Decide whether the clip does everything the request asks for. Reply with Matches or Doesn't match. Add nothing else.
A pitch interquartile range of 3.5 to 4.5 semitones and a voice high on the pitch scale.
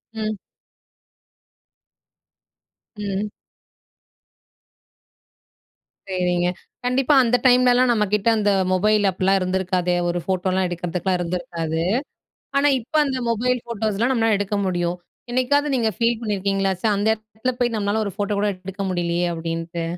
Matches